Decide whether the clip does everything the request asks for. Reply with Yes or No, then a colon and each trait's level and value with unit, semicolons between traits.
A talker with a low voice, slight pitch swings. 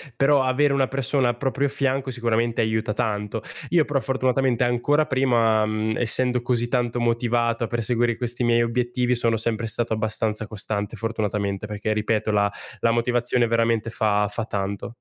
Yes: low, 115 Hz; narrow, 2.2 semitones